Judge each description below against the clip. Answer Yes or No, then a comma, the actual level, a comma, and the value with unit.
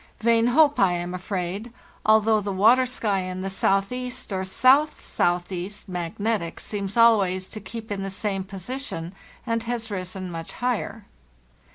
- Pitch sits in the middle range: No, high, 200 Hz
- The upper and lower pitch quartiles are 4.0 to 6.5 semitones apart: No, average, 3.6 semitones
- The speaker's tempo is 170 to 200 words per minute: No, average, 155 wpm